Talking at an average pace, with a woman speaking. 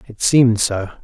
No: average, 175 wpm; male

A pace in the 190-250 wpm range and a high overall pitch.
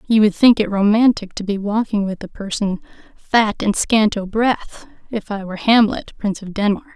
Yes: average, 200 wpm; high, 210 Hz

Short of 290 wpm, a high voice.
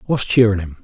No: fast, 215 wpm; low, 105 Hz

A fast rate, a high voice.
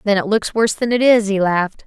Yes: fast, 290 wpm; high, 210 Hz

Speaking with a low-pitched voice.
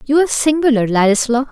No: very high, 260 Hz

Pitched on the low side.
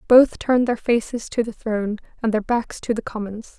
No: high, 225 Hz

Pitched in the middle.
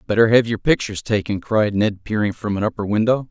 No: low, 105 Hz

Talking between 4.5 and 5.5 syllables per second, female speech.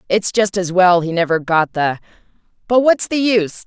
Yes: 5.0 syllables/s; female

